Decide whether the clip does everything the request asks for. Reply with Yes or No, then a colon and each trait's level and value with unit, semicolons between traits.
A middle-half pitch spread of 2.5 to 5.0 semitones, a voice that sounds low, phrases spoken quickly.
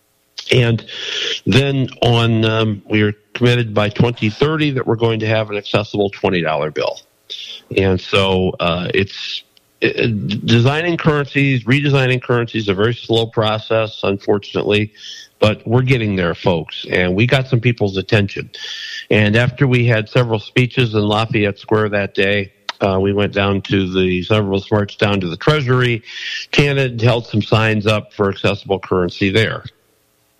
No: average, 3.5 semitones; low, 110 Hz; average, 150 wpm